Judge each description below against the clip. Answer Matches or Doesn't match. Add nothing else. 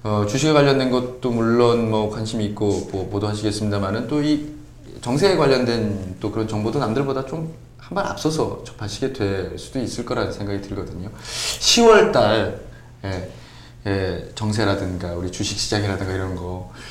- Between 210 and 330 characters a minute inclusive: Matches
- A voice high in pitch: Doesn't match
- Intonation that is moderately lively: Matches